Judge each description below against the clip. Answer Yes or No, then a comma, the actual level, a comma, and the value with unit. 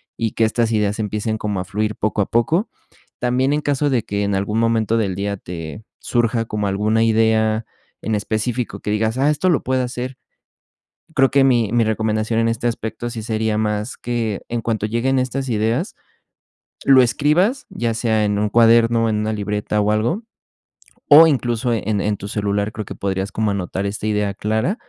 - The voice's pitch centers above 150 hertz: No, low, 110 Hz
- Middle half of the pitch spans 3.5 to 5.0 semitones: No, narrow, 2.4 semitones